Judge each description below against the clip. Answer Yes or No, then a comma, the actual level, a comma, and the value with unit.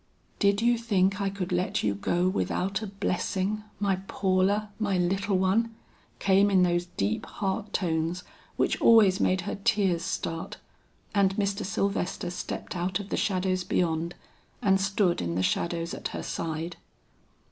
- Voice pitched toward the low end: No, high, 190 Hz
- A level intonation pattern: Yes, narrow, 2.3 semitones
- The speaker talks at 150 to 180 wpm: Yes, average, 155 wpm